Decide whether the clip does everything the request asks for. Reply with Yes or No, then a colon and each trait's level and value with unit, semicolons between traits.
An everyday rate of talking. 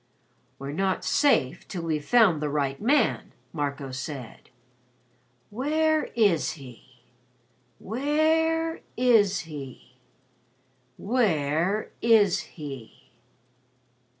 No: slow, 85 wpm